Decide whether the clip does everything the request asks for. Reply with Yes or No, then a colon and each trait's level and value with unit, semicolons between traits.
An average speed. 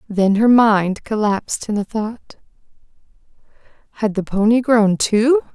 No: slow, 120 wpm